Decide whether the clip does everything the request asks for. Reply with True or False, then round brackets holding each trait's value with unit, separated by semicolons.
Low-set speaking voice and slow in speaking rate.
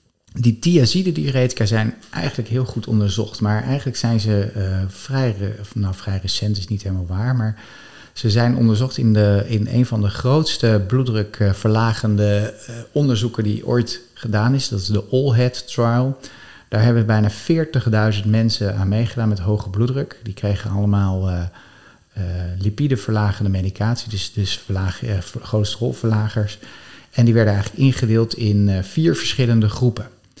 False (110 Hz; 155 wpm)